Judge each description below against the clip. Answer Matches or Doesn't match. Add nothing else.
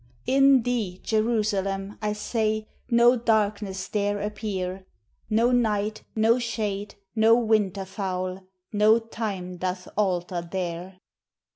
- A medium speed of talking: Doesn't match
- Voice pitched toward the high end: Matches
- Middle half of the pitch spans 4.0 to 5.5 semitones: Doesn't match